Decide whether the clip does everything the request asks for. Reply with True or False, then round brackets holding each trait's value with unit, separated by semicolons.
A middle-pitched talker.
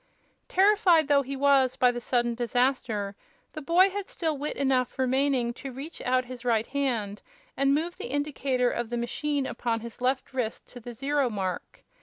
False (260 Hz)